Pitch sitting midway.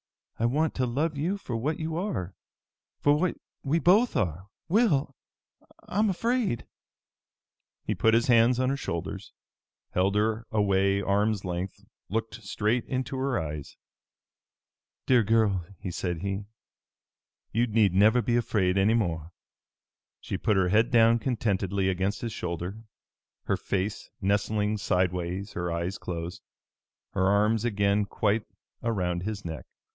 No: low, 105 Hz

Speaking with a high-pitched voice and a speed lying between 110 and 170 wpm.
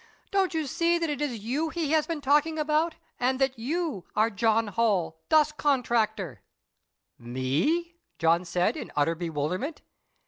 Yes: very high, 255 Hz; average, 150 wpm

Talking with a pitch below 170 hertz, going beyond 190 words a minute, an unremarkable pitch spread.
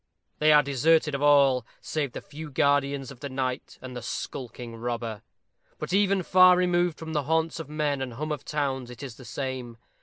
Yes: medium, 140 Hz; average, 200 wpm; average, 3.3 semitones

